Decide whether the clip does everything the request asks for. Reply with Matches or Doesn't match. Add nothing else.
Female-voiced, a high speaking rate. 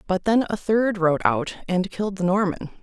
Matches